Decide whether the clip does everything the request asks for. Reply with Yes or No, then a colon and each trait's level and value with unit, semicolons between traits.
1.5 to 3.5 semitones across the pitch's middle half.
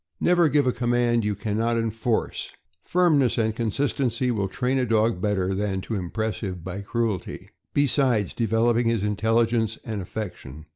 Yes: average, 2.8 semitones